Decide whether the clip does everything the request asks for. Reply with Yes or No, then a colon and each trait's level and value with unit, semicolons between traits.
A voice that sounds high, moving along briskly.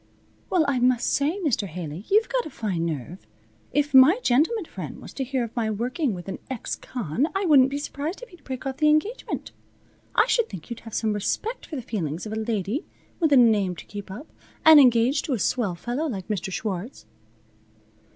Yes: high, 245 Hz; fast, 210 wpm